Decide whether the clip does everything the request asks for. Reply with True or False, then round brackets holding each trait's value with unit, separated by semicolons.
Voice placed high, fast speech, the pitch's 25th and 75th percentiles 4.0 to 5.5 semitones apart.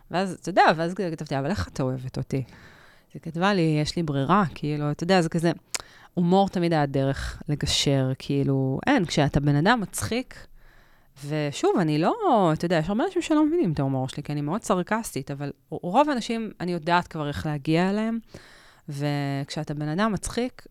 False (155 Hz; 180 wpm; 4.8 semitones)